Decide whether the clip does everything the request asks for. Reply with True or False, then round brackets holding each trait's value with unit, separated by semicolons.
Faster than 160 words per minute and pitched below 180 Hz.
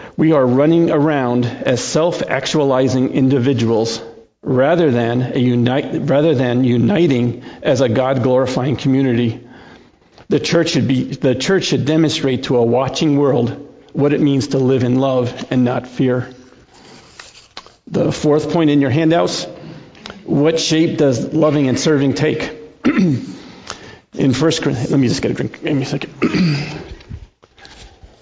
False (140 wpm; 135 Hz)